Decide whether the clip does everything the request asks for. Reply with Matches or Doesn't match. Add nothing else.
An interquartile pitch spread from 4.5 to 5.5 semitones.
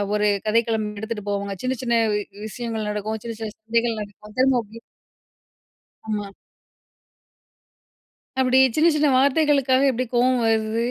Doesn't match